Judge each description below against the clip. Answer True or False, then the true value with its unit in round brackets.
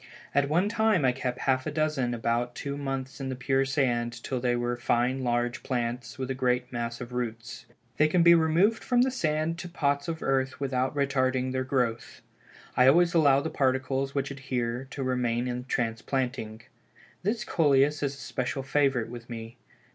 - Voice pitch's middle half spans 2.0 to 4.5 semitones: True (2.7 semitones)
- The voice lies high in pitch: False (130 Hz)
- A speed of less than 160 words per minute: False (185 wpm)